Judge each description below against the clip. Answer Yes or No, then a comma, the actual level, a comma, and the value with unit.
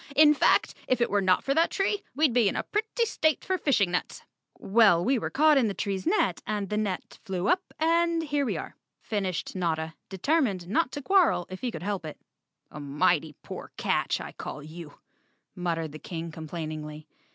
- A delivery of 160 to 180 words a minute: No, average, 195 wpm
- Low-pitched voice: No, high, 200 Hz